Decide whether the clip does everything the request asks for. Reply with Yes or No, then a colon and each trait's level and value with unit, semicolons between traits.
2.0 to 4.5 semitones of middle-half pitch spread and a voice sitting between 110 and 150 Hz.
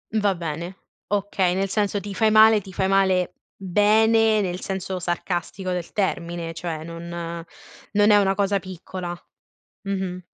No: average, 2.7 semitones; high, 190 Hz